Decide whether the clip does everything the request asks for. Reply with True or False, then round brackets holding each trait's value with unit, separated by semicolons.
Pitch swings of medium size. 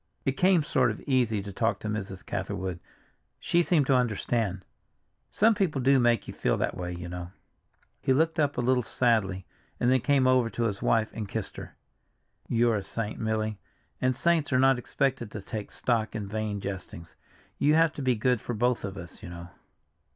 True (4.4 semitones)